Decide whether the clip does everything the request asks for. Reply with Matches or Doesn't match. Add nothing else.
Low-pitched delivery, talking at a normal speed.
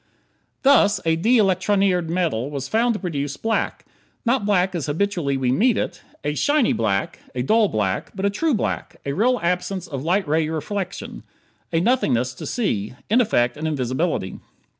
Doesn't match